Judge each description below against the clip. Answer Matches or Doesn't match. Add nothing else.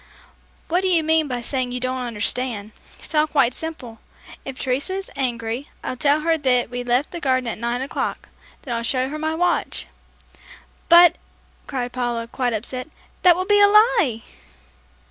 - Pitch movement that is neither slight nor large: Matches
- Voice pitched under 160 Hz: Doesn't match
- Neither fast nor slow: Matches